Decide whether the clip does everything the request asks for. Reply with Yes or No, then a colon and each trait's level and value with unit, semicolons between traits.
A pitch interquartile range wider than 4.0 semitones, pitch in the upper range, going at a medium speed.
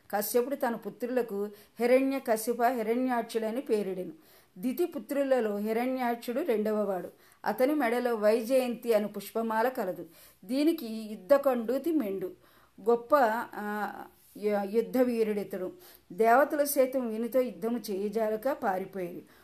No: average, 3.6 semitones; high, 230 Hz; average, 95 wpm